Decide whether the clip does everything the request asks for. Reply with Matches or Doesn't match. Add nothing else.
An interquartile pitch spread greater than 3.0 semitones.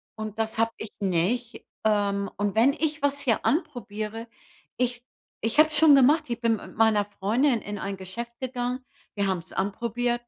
Matches